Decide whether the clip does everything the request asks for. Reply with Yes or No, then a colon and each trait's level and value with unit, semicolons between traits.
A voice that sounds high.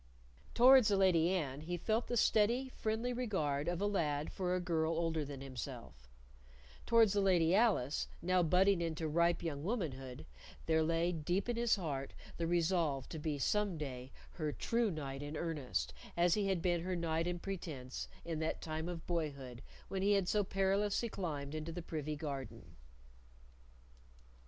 No: medium, 170 Hz